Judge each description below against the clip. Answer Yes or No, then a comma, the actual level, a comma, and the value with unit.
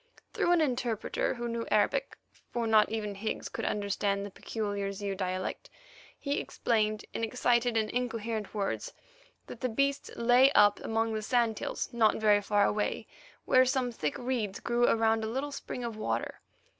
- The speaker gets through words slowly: No, average, 170 wpm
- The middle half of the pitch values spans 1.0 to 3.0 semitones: Yes, average, 2.7 semitones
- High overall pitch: Yes, high, 225 Hz